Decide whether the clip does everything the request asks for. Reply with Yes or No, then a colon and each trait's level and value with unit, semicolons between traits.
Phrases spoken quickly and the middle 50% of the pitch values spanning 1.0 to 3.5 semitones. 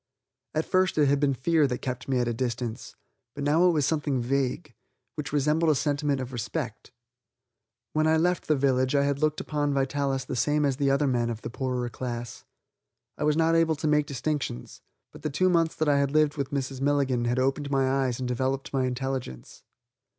Yes: fast, 210 wpm; average, 2.7 semitones